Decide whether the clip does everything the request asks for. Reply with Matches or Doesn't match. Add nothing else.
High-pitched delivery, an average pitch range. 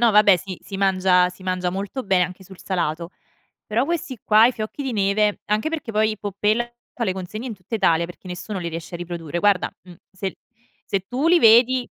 Matches